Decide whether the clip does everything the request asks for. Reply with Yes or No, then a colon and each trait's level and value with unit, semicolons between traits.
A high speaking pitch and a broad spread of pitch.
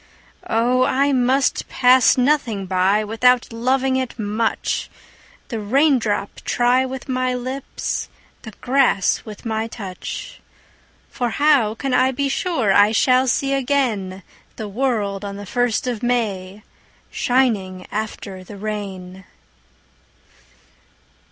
No: high, 235 Hz; average, 4.1 semitones